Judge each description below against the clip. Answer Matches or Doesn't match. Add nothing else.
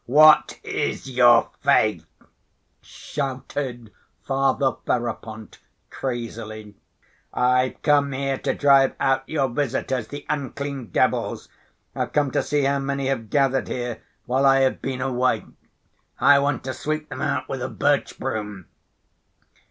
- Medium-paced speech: Doesn't match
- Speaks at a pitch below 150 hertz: Matches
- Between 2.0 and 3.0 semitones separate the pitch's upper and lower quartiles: Matches